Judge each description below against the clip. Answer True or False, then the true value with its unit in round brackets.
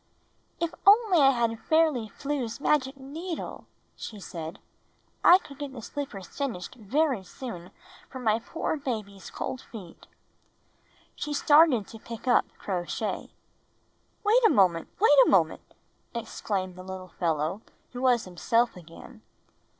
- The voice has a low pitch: False (235 Hz)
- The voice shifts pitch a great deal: True (7.2 semitones)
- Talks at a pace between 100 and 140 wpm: True (135 wpm)